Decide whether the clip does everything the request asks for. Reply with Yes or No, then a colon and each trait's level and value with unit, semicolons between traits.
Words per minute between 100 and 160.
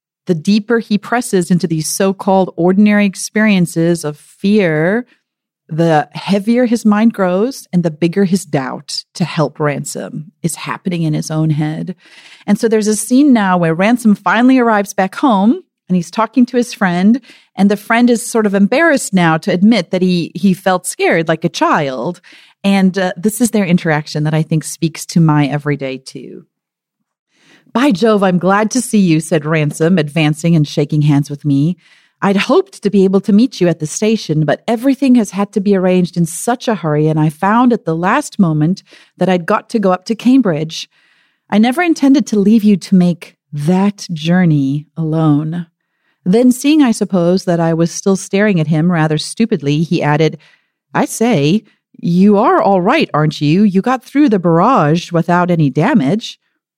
No: average, 185 wpm